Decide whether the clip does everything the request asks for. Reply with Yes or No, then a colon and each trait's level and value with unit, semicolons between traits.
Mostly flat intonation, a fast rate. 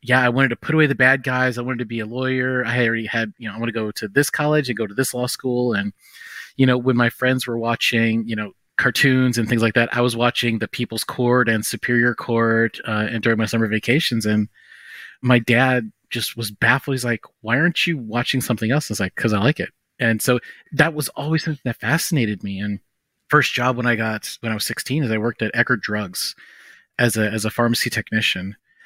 Yes: narrow, 2.3 semitones; fast, 240 wpm